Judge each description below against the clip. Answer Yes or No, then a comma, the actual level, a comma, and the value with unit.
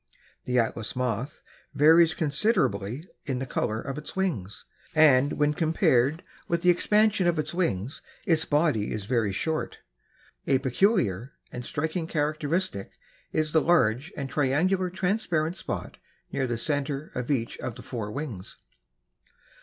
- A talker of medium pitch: Yes, medium, 150 Hz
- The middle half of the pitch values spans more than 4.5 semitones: Yes, average, 5.2 semitones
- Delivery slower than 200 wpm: Yes, average, 140 wpm